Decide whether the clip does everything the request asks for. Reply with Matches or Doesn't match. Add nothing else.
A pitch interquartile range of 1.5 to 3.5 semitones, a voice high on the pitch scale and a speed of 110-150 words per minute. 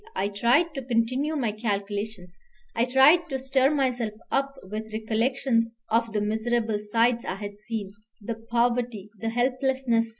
Matches